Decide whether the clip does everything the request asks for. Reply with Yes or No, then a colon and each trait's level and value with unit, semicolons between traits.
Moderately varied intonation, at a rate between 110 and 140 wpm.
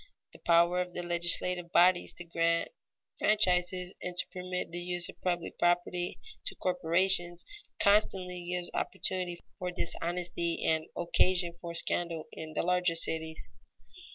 No: narrow, 1.0 semitones; slow, 135 wpm